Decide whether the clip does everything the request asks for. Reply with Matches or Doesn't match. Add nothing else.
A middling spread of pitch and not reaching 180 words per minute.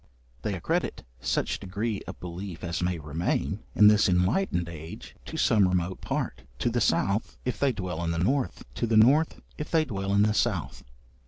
Doesn't match